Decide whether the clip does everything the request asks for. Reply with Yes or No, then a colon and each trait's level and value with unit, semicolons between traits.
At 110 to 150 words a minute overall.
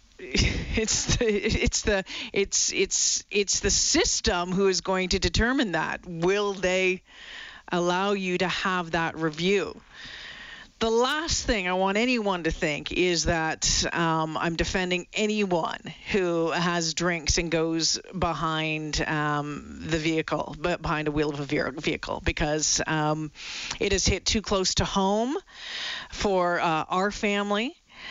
Yes: average, 140 wpm